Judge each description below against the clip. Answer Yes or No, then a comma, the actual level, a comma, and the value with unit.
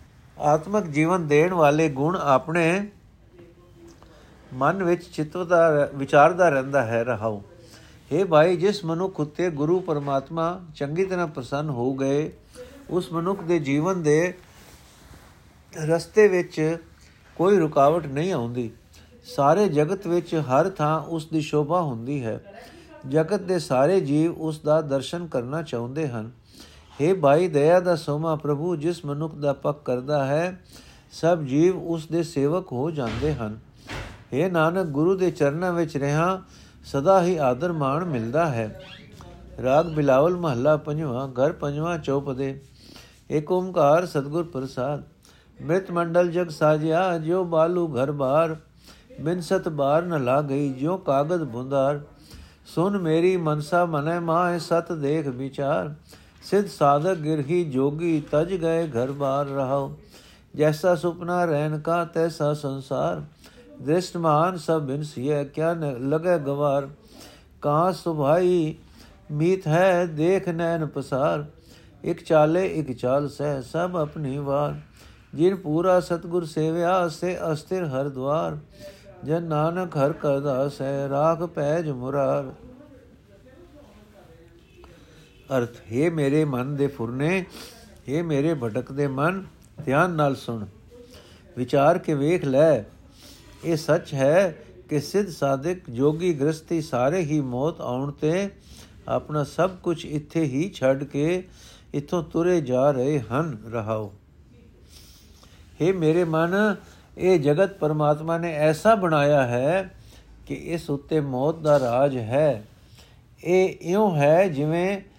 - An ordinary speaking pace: Yes, average, 125 wpm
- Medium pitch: Yes, medium, 155 Hz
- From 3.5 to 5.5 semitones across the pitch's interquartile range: Yes, average, 3.8 semitones